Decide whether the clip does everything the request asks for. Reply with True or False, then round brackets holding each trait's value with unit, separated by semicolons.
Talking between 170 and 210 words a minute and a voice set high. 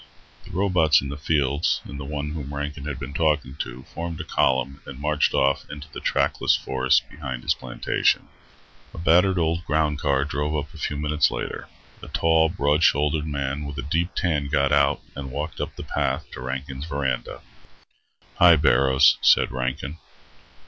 False (175 wpm; 75 Hz)